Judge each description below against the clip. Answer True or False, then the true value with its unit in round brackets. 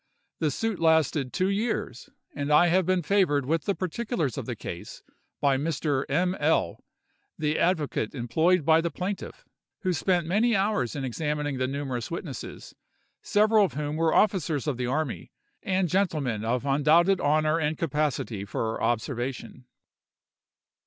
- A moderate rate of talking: True (150 wpm)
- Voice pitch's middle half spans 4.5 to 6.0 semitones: True (5.0 semitones)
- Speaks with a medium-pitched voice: True (155 Hz)